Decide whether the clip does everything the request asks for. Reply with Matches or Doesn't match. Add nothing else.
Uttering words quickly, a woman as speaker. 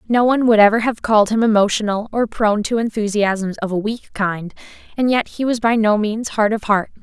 Matches